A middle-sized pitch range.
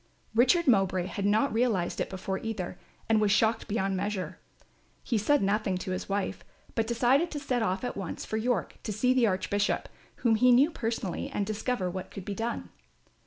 Yes: average, 3.8 semitones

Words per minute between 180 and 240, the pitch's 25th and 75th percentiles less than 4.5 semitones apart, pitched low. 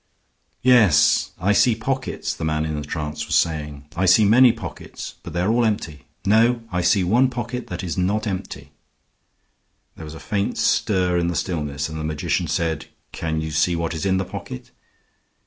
No: average, 190 wpm; average, 5.3 semitones; very low, 90 Hz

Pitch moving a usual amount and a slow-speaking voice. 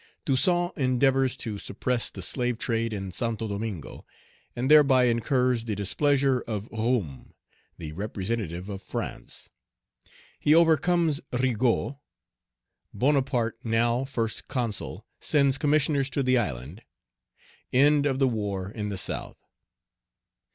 Yes: average, 4.3 semitones; slow, 115 wpm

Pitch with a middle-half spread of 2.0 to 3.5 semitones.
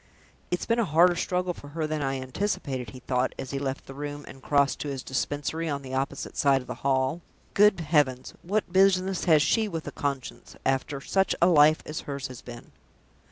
No: average, 4.5 semitones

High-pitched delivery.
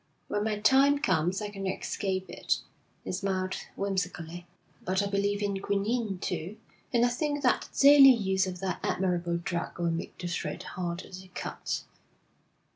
Yes: high, 195 Hz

